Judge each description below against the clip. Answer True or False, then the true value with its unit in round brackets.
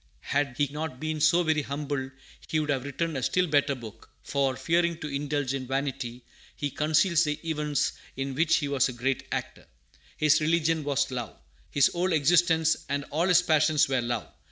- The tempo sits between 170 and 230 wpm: True (185 wpm)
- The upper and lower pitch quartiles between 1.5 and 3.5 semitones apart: True (2.8 semitones)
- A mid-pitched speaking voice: True (145 Hz)